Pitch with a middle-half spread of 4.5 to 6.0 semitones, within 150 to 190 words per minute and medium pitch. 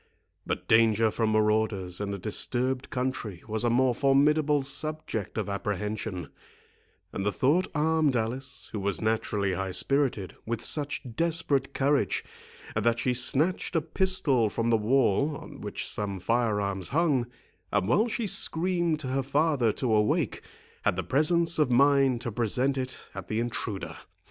No: average, 5.1 semitones; average, 155 wpm; low, 120 Hz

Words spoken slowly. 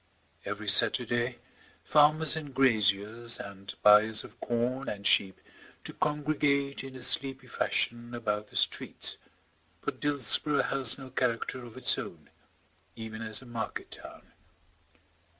Yes: slow, 130 wpm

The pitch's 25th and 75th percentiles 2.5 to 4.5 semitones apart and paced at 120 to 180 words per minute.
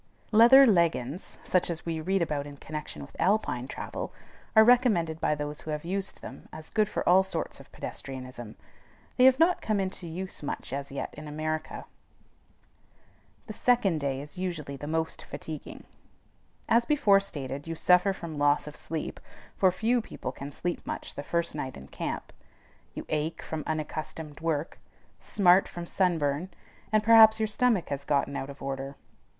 No: average, 5.1 semitones; average, 170 wpm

